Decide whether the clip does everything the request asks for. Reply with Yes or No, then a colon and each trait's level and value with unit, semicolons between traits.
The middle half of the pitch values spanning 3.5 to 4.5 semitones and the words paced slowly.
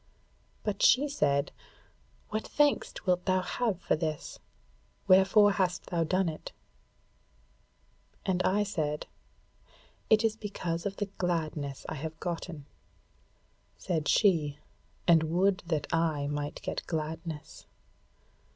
Yes: average, 4.0 semitones; slow, 115 wpm